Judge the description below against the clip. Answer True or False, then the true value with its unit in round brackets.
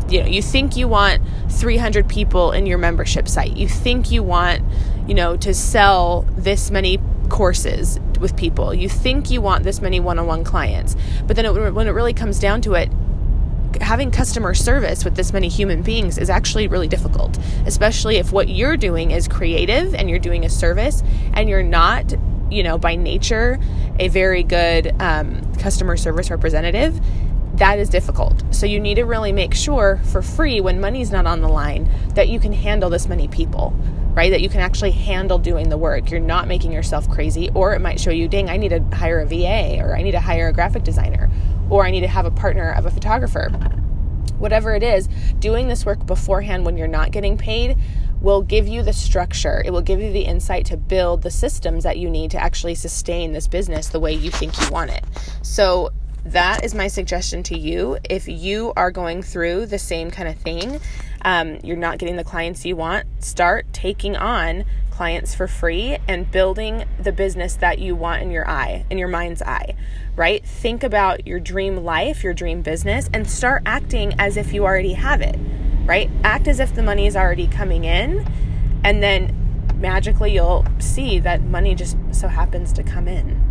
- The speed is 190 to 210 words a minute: True (200 wpm)